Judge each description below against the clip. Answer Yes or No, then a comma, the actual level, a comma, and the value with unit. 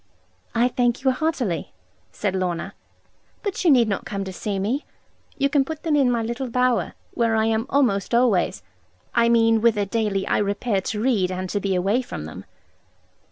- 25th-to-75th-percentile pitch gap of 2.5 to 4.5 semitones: Yes, average, 4.1 semitones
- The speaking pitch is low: No, high, 225 Hz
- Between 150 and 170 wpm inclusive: No, average, 185 wpm